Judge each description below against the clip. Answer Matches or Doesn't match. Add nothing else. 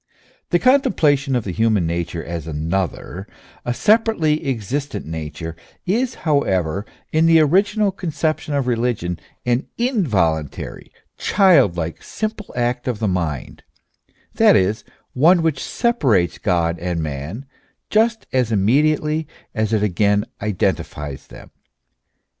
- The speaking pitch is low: Matches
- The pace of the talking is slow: Matches